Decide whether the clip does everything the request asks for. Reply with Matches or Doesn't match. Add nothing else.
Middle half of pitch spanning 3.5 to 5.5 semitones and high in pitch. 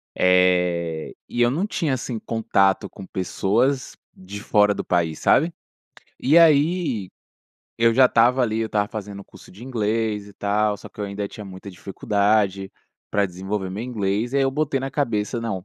Doesn't match